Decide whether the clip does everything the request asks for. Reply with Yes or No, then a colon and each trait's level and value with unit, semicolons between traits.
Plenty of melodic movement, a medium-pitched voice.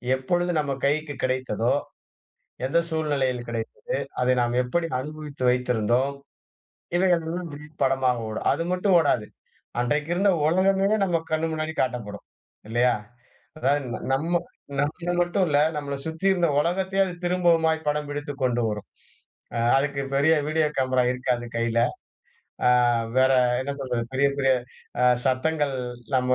No: average, 4.2 semitones; medium, 145 Hz